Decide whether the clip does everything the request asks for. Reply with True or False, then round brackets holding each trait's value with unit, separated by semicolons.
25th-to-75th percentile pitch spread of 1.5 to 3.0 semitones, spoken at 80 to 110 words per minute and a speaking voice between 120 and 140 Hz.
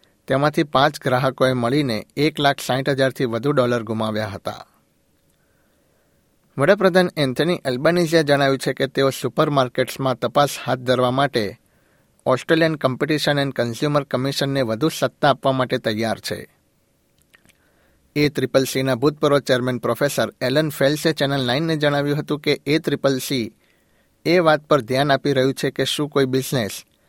False (2.4 semitones; 135 wpm; 135 Hz)